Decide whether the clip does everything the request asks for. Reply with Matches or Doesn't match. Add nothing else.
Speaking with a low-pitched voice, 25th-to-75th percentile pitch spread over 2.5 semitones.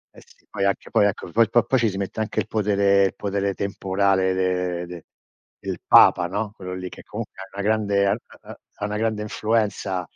Doesn't match